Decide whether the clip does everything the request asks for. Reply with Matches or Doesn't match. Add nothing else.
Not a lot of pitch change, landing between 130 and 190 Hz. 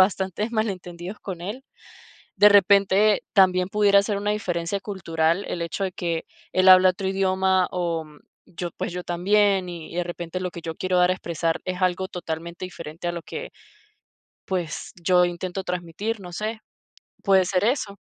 Matches